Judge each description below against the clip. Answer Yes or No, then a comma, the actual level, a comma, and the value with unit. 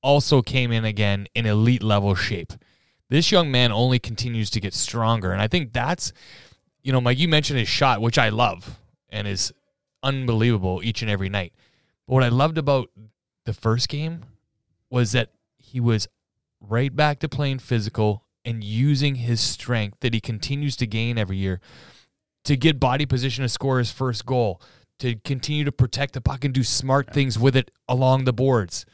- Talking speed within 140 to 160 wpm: No, average, 185 wpm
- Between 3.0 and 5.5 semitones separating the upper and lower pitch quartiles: Yes, average, 3.5 semitones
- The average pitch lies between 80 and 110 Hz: No, low, 120 Hz